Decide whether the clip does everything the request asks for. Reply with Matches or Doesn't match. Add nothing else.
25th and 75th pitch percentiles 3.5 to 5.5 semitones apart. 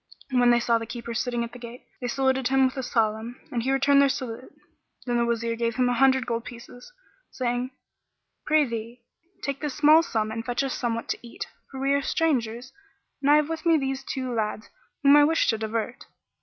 Doesn't match